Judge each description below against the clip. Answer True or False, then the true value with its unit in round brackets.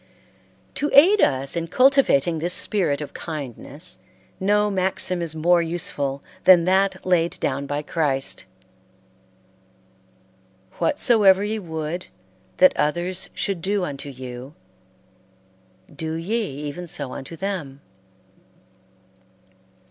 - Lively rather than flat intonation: False (4.9 semitones)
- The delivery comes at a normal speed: False (105 wpm)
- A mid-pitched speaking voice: True (170 Hz)